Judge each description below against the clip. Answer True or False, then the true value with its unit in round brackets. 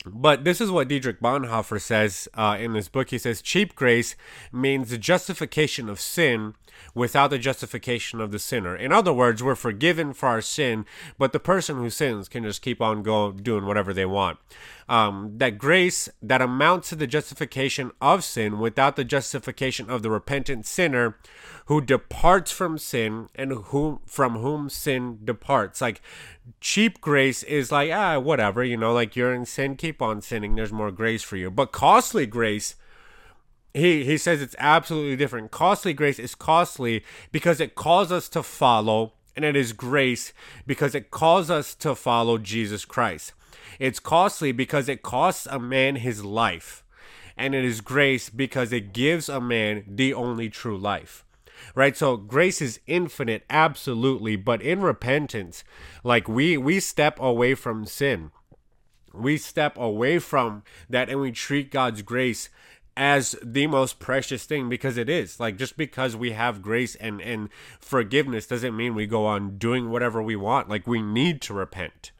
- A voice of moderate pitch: False (125 Hz)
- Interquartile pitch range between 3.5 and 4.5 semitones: True (4.1 semitones)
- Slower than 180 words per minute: True (170 wpm)